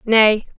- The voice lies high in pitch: Yes, high, 220 Hz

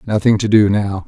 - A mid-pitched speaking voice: No, low, 105 Hz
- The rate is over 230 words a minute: No, fast, 225 wpm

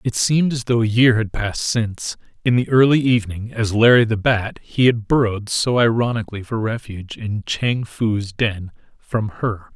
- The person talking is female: No, male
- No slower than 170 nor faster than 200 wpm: Yes, average, 180 wpm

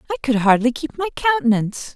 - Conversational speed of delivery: Yes, average, 185 wpm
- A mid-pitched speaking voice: No, very high, 275 Hz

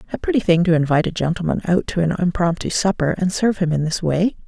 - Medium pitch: Yes, medium, 175 Hz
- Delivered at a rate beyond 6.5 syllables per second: Yes, 6.7 syllables/s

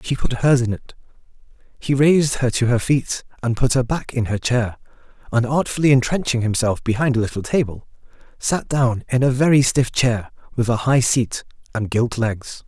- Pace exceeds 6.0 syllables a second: No, 5.0 syllables/s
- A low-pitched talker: Yes, low, 125 Hz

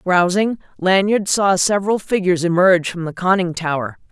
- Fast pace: No, average, 145 wpm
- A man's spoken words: No, female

